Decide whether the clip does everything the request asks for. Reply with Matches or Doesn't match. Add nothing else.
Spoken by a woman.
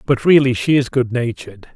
Doesn't match